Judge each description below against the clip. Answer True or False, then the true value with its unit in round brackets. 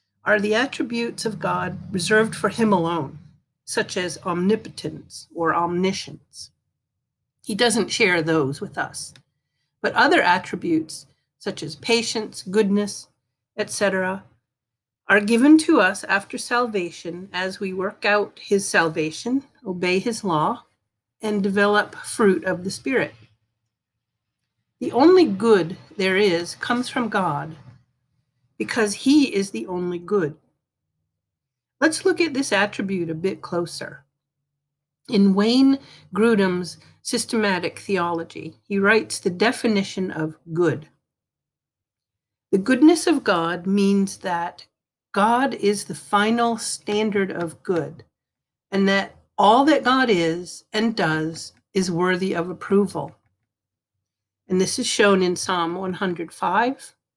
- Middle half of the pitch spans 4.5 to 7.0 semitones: True (5.1 semitones)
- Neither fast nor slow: False (120 wpm)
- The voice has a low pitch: False (190 Hz)